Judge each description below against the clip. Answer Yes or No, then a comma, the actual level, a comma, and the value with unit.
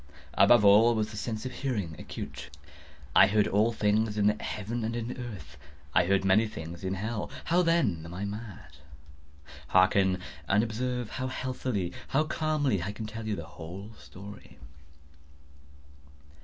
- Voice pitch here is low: Yes, low, 105 Hz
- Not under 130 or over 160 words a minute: Yes, average, 155 wpm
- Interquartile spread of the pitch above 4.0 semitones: No, average, 3.5 semitones